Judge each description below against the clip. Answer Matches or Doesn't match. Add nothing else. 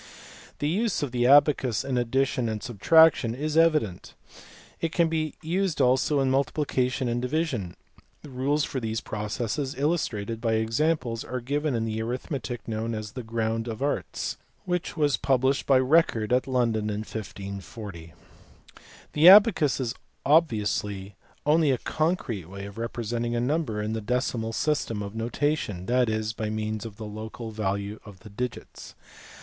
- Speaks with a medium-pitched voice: Doesn't match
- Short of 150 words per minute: Doesn't match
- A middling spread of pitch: Matches